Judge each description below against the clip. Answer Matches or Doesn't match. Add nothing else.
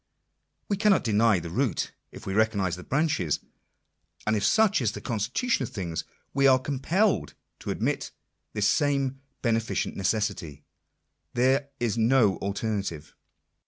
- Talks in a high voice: Doesn't match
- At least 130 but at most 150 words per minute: Matches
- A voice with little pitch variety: Doesn't match